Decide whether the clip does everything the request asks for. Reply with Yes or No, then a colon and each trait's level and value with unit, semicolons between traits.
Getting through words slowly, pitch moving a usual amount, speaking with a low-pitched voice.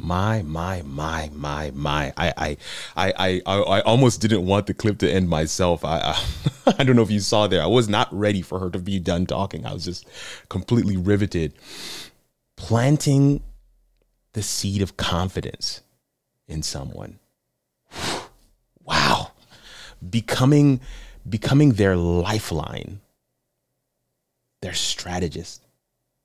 Yes: slow, 130 wpm; average, 4.6 semitones; low, 100 Hz